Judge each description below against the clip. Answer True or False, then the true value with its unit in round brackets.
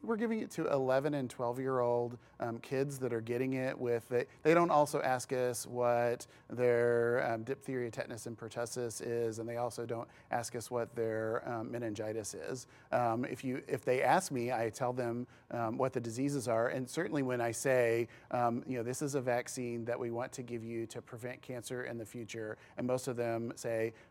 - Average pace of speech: False (210 wpm)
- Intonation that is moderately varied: False (1.7 semitones)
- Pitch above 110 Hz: True (120 Hz)